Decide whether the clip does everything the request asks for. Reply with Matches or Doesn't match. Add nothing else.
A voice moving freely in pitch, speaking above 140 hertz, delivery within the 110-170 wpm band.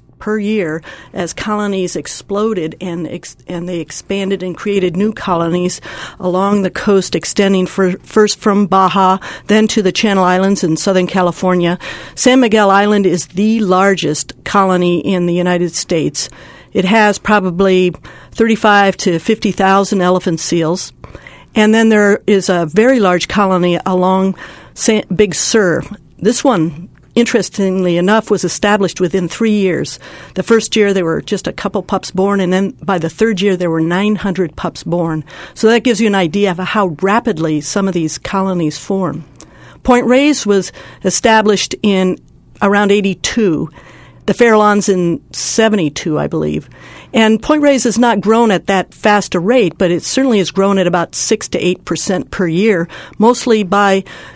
Doesn't match